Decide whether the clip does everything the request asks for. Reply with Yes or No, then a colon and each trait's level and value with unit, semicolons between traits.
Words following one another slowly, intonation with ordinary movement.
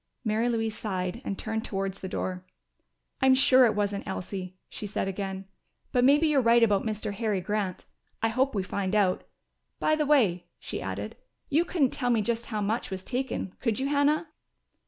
No: average, 185 wpm; average, 4.7 semitones